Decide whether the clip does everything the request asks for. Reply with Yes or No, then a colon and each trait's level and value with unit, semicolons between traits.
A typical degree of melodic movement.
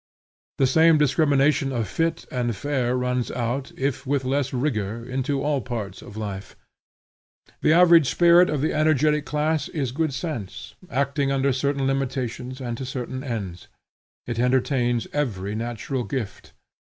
Yes: average, 3.2 semitones